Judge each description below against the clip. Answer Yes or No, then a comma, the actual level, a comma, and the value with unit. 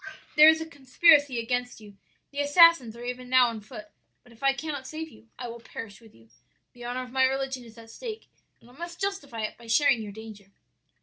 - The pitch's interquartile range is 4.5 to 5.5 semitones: No, average, 4.0 semitones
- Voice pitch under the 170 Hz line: No, very high, 250 Hz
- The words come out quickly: Yes, fast, 220 wpm